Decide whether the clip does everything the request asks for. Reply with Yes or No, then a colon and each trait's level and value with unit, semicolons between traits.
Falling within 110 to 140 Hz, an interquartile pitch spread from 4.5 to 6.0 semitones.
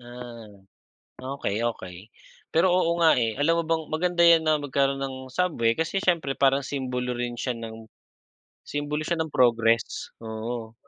Yes: low, 135 Hz; wide, 5.5 semitones